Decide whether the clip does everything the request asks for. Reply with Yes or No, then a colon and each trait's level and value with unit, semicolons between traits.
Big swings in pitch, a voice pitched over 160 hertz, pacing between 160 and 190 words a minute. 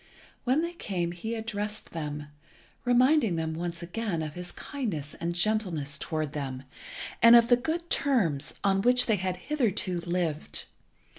No: wide, 6.3 semitones; medium, 185 Hz; average, 150 wpm